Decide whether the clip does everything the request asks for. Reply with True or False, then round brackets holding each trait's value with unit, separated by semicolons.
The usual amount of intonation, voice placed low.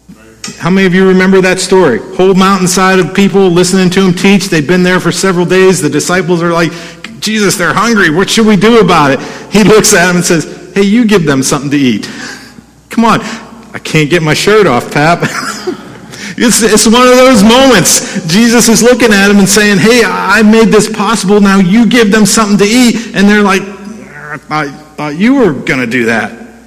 False (3.4 semitones; 195 Hz)